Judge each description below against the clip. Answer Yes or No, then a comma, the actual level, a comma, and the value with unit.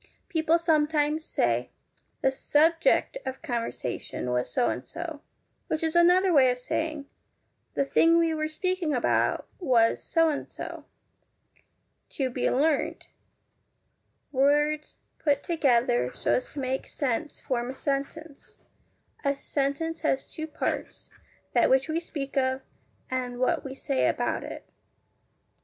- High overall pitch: Yes, very high, 290 Hz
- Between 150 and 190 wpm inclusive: No, average, 140 wpm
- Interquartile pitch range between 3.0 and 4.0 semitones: Yes, average, 3.5 semitones